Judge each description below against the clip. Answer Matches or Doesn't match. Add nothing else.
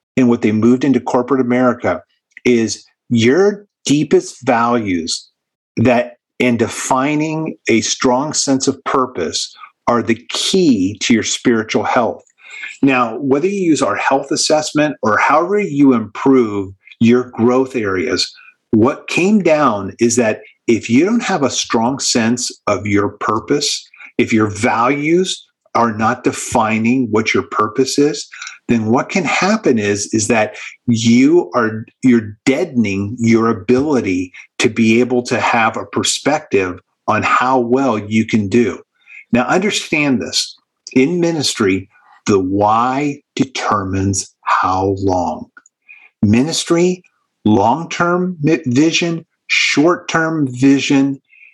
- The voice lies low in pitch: Matches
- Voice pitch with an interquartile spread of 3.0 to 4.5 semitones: Doesn't match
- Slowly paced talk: Matches